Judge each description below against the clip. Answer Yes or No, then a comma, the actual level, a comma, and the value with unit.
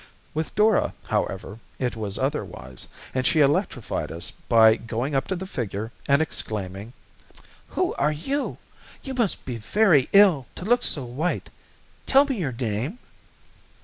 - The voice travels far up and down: Yes, wide, 8.9 semitones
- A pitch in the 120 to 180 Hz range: Yes, low, 135 Hz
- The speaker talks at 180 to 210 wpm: No, average, 145 wpm